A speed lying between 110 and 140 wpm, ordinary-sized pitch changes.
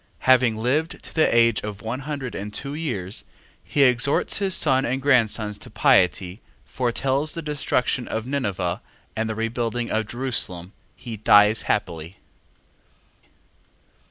Yes: slow, 135 wpm; average, 4.2 semitones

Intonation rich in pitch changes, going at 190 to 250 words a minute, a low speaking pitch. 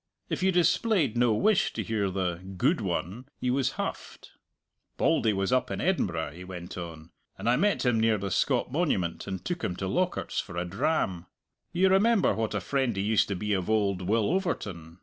Yes: wide, 8.2 semitones; average, 200 wpm; low, 110 Hz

